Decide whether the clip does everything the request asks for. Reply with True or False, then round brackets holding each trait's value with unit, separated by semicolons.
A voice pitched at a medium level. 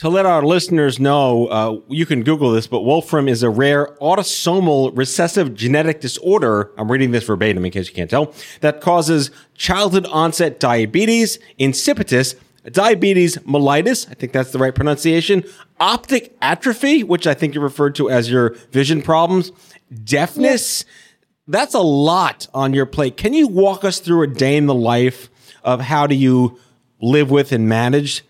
True (145 Hz)